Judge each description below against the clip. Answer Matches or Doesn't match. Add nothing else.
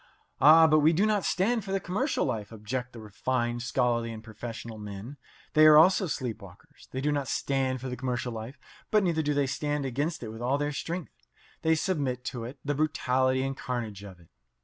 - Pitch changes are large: Doesn't match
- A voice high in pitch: Doesn't match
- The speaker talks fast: Matches